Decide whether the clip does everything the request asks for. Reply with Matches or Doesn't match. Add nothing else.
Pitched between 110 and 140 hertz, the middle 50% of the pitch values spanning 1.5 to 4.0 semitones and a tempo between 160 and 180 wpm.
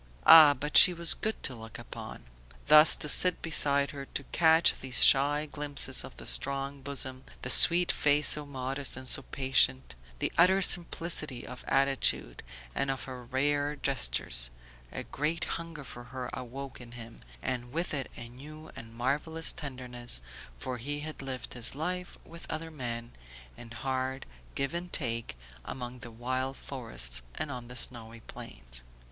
Matches